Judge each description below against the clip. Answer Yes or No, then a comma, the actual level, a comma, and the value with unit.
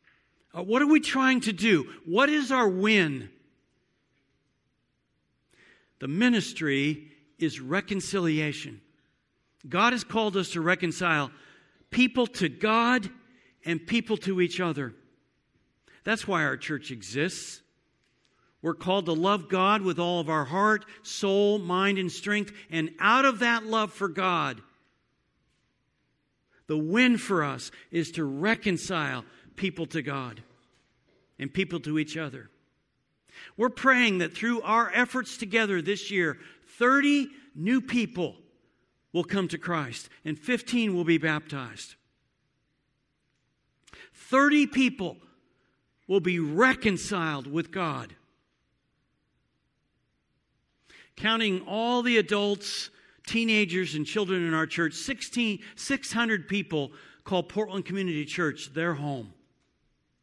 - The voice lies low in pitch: No, medium, 185 Hz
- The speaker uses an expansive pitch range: Yes, wide, 5.8 semitones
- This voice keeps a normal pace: No, slow, 115 wpm